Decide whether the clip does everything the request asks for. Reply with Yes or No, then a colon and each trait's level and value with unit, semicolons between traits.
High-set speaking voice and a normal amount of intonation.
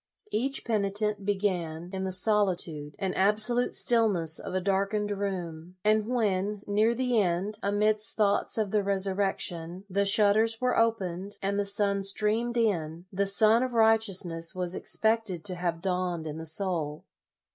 Yes: high, 200 Hz; average, 3.0 semitones